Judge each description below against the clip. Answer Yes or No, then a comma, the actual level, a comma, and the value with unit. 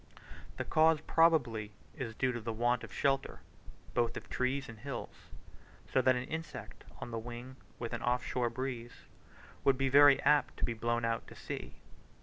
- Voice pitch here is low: Yes, low, 125 Hz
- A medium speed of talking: Yes, average, 180 wpm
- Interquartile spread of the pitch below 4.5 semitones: Yes, average, 2.7 semitones